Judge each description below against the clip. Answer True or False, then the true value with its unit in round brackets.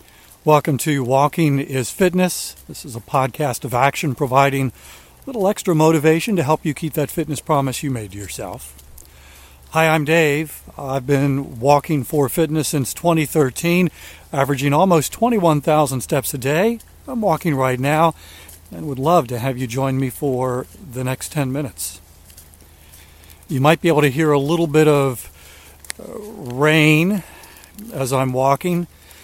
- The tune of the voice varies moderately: True (3.8 semitones)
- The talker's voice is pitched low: False (145 Hz)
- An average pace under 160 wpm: True (150 wpm)